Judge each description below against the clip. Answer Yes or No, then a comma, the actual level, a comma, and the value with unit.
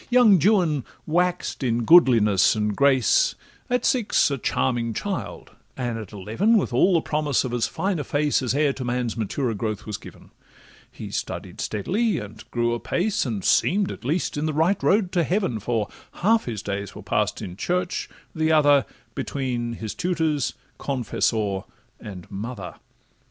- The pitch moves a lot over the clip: Yes, wide, 7.8 semitones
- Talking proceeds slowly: No, average, 165 wpm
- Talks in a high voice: No, low, 135 Hz